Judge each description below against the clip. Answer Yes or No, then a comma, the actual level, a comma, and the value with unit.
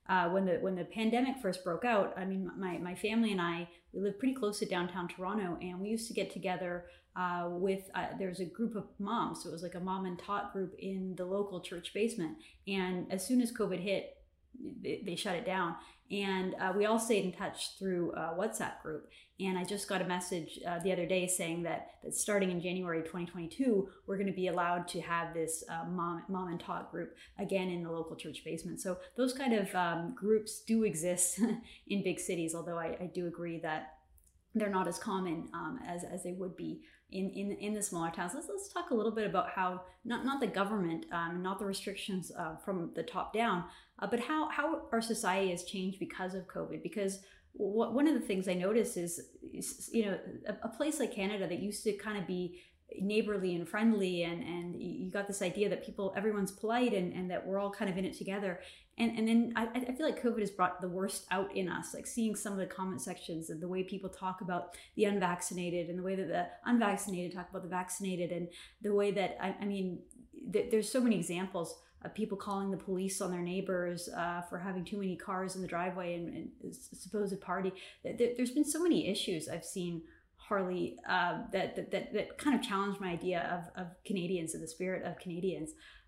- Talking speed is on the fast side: Yes, fast, 225 wpm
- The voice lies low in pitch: No, high, 190 Hz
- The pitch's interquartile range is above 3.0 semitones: No, average, 2.7 semitones